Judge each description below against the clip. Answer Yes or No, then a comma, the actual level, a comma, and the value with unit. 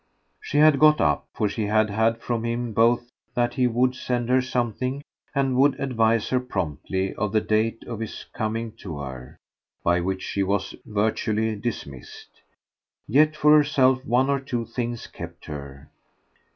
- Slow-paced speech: No, average, 165 wpm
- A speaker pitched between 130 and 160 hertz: No, low, 115 Hz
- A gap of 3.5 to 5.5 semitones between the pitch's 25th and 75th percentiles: Yes, average, 3.9 semitones